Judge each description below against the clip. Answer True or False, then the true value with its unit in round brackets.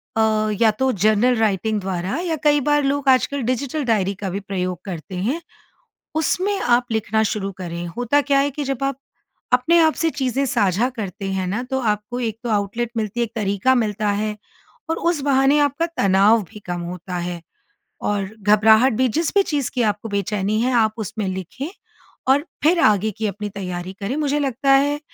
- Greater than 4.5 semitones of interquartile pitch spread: True (5.4 semitones)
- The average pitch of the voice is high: True (220 Hz)